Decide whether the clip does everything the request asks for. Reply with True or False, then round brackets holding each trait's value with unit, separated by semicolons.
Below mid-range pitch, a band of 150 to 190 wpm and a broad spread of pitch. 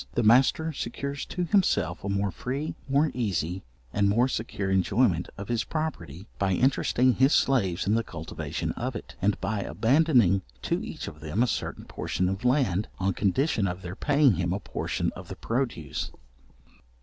True (110 Hz; 175 wpm; 5.7 semitones)